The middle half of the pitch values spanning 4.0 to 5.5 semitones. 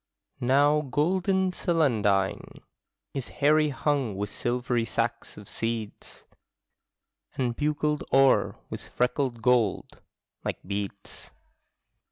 Yes: average, 4.6 semitones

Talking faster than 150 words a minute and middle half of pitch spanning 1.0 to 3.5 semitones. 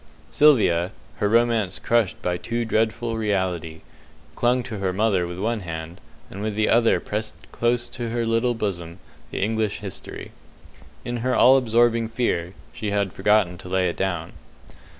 No: average, 160 wpm; average, 4.0 semitones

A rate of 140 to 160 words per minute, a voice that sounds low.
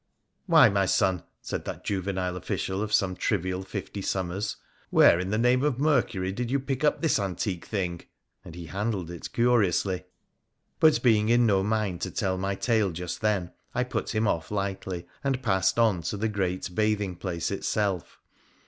No: average, 185 wpm; low, 100 Hz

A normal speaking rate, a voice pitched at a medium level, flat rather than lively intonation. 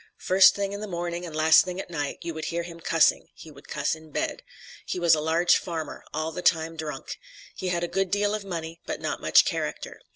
No: fast, 235 wpm; medium, 170 Hz; narrow, 2.3 semitones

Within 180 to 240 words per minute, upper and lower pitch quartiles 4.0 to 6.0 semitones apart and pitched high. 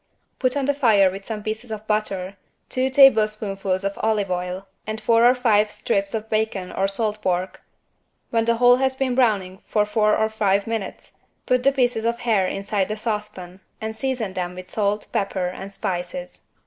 No: average, 185 wpm; average, 3.0 semitones; high, 215 Hz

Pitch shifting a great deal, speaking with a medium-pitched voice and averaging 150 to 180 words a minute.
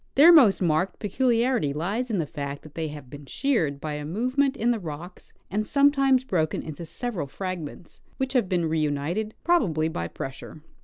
Yes: wide, 8.1 semitones; medium, 180 Hz; average, 175 wpm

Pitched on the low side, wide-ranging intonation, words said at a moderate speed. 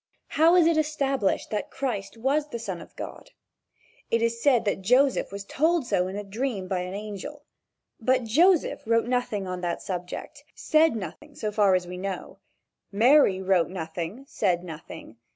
No: high, 215 Hz; wide, 6.4 semitones; average, 170 wpm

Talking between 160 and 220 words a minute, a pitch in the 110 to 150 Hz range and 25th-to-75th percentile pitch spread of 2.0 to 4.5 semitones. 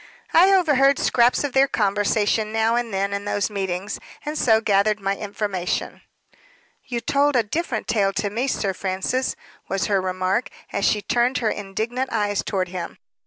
No: average, 165 wpm; high, 215 Hz; average, 3.8 semitones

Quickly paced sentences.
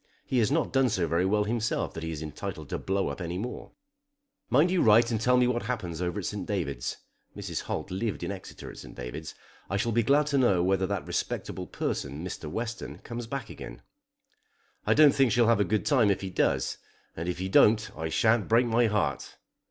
Yes: fast, 215 wpm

